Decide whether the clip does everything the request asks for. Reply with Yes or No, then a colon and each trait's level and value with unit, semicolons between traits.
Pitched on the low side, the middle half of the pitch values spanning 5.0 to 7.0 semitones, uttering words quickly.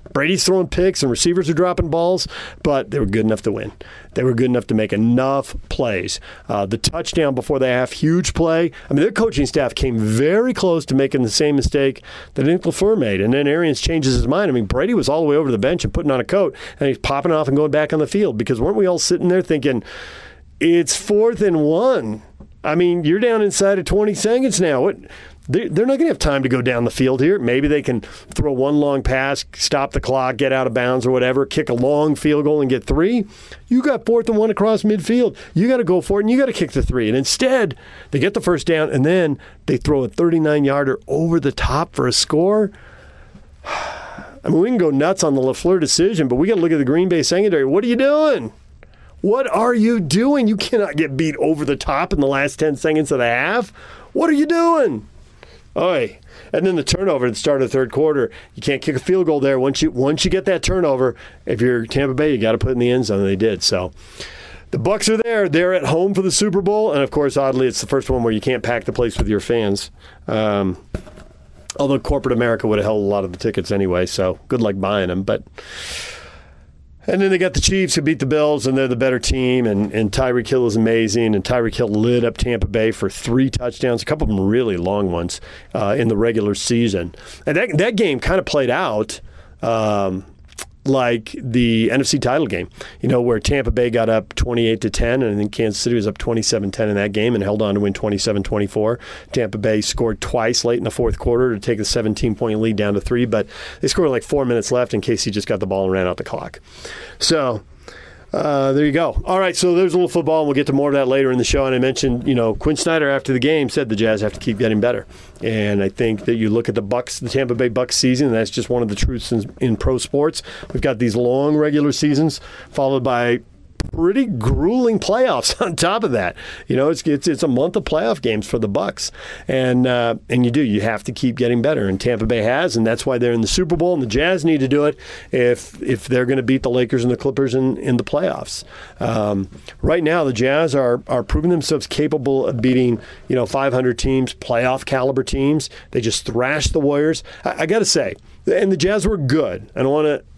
Yes: low, 130 Hz; average, 5.3 semitones; fast, 245 wpm